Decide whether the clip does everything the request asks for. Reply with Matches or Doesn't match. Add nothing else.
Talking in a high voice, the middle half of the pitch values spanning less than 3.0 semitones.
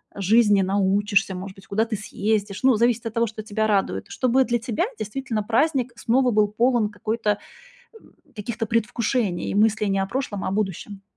Matches